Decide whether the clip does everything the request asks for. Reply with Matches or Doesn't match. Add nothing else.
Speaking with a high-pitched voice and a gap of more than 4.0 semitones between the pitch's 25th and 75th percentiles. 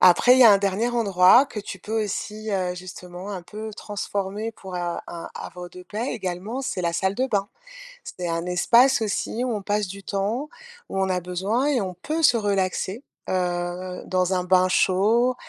Doesn't match